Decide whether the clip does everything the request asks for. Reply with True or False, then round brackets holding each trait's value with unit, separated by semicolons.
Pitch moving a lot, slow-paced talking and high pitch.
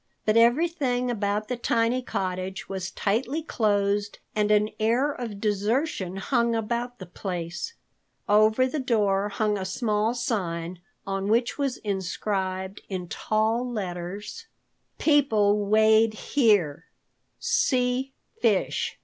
False (3.8 semitones; 115 wpm; 215 Hz)